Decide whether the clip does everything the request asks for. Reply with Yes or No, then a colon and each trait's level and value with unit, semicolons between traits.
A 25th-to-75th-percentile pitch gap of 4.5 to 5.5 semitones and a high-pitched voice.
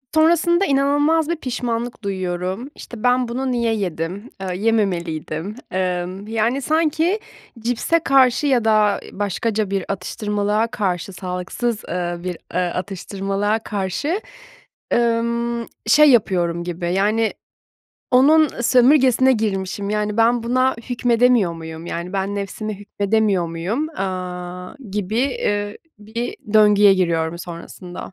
Yes: average, 4.8 semitones; high, 210 Hz